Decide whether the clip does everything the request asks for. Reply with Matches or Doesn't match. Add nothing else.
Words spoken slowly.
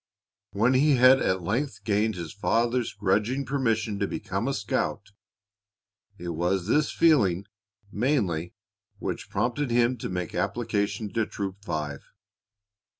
Matches